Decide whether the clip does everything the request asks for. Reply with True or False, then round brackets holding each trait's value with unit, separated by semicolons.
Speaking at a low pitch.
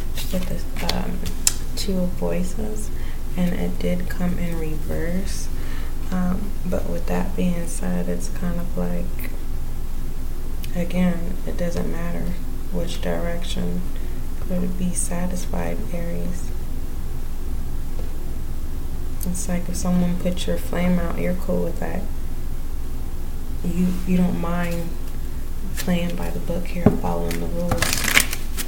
True (80 Hz)